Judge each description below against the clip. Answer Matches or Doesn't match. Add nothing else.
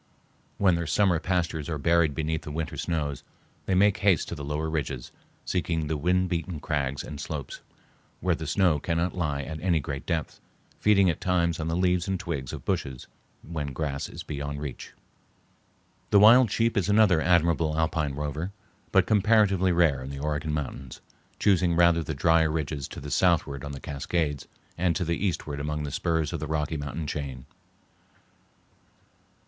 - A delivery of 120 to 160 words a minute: Doesn't match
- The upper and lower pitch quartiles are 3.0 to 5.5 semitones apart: Matches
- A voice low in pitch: Matches